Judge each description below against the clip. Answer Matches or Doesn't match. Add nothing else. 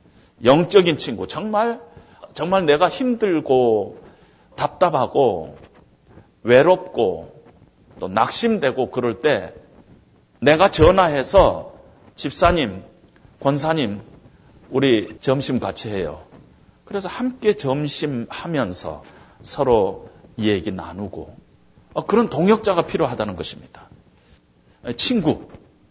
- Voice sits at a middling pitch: Matches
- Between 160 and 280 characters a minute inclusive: Matches